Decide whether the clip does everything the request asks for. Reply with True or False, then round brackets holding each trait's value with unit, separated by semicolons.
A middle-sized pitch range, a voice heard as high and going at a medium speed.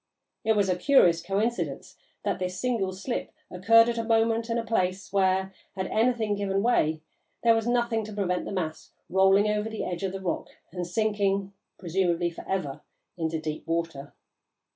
True (3.8 semitones; 195 Hz; 175 wpm)